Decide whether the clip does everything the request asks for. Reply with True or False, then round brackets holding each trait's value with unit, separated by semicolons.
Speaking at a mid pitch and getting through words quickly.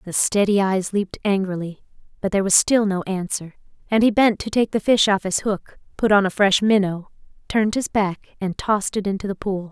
False (200 Hz; 215 wpm)